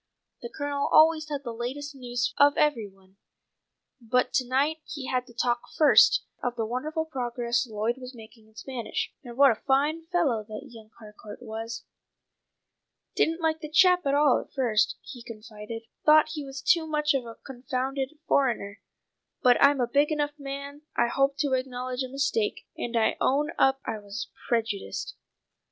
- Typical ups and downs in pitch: Yes, average, 3.7 semitones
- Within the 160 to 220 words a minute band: Yes, average, 175 wpm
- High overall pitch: Yes, very high, 260 Hz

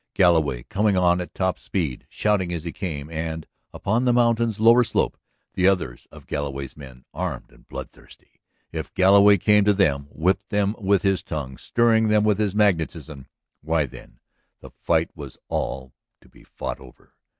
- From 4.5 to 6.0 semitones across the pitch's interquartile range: Yes, wide, 5.5 semitones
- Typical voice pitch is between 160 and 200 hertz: No, very low, 90 Hz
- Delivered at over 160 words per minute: Yes, average, 170 wpm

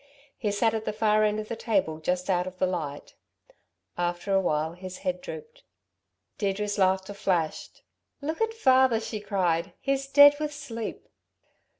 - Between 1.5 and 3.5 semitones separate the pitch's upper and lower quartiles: No, average, 5.0 semitones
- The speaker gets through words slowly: No, average, 165 wpm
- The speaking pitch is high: Yes, high, 205 Hz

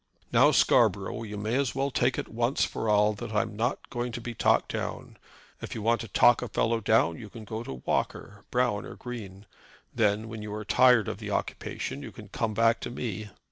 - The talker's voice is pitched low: Yes, low, 110 Hz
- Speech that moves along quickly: Yes, fast, 220 wpm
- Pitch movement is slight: Yes, narrow, 2.3 semitones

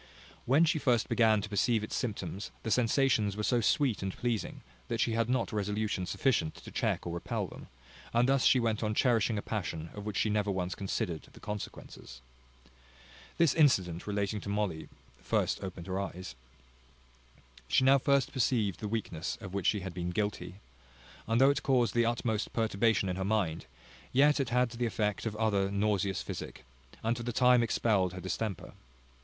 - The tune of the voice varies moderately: Yes, average, 3.6 semitones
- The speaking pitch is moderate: No, low, 105 Hz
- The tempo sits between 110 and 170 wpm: No, average, 185 wpm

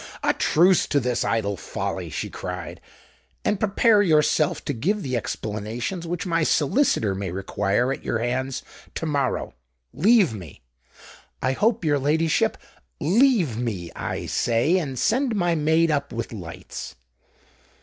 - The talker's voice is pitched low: No, medium, 145 Hz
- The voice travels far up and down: Yes, wide, 7.3 semitones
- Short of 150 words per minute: Yes, average, 140 wpm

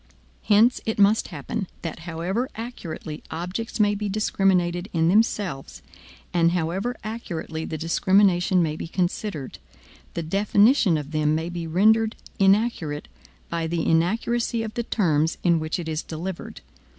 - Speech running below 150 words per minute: Yes, average, 140 wpm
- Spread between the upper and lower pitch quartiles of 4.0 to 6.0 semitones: Yes, average, 4.5 semitones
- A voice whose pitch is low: No, medium, 180 Hz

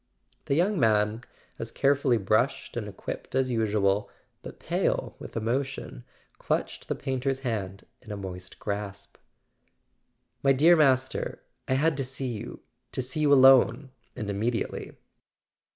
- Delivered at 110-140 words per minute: Yes, slow, 135 wpm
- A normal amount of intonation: Yes, average, 4.4 semitones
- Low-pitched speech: Yes, low, 125 Hz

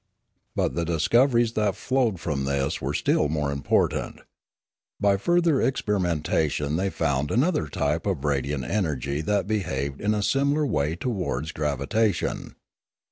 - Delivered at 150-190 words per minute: No, slow, 135 wpm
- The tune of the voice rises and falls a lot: Yes, wide, 7.1 semitones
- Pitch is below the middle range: Yes, very low, 85 Hz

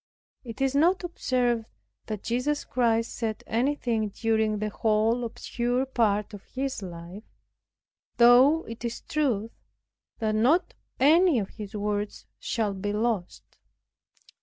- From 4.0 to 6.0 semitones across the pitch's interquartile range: No, average, 3.3 semitones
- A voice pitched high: Yes, high, 230 Hz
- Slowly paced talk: Yes, slow, 125 wpm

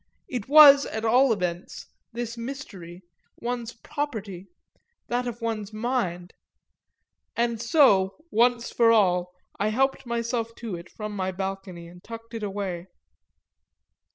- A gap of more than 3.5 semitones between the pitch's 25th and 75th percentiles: Yes, average, 3.9 semitones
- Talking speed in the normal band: No, slow, 125 wpm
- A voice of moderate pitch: No, high, 225 Hz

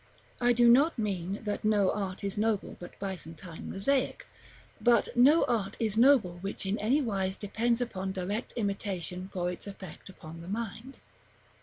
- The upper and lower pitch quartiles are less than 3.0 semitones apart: No, average, 3.8 semitones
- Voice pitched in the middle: No, high, 205 Hz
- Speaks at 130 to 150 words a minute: No, average, 160 wpm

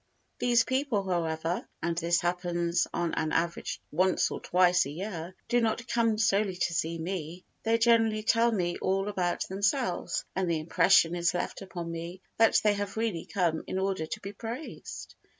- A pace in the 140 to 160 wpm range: No, average, 175 wpm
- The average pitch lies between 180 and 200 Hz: Yes, medium, 185 Hz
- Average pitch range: Yes, average, 4.0 semitones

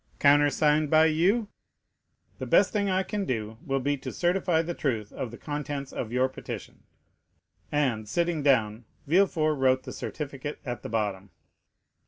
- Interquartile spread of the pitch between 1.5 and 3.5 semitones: No, average, 4.3 semitones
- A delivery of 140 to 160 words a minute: Yes, average, 155 wpm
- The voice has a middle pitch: Yes, medium, 145 Hz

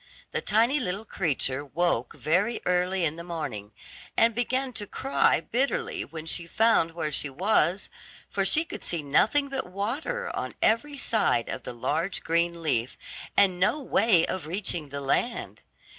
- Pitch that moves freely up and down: Yes, wide, 6.5 semitones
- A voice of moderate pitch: Yes, medium, 180 Hz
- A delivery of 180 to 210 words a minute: No, average, 160 wpm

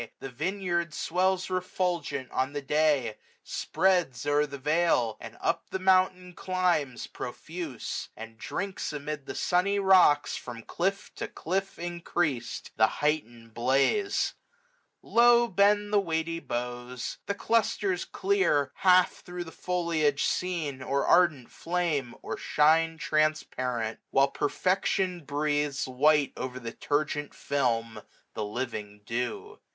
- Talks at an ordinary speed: No, slow, 130 wpm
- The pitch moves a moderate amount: No, wide, 5.7 semitones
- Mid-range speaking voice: Yes, medium, 155 Hz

